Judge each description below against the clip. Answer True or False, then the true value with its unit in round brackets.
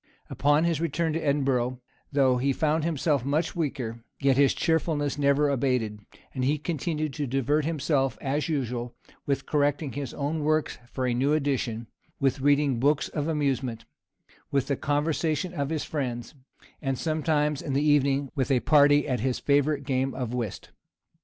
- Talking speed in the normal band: True (165 wpm)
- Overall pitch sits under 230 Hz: True (140 Hz)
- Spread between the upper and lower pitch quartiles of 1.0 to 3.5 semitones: True (2.4 semitones)